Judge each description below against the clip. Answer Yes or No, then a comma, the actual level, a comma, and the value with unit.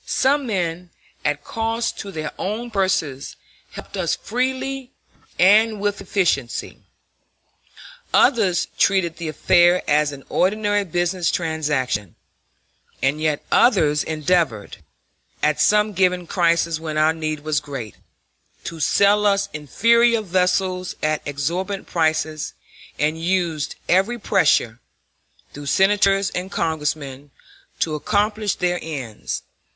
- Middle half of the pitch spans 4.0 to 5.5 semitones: Yes, average, 4.7 semitones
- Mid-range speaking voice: Yes, medium, 175 Hz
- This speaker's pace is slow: Yes, slow, 115 wpm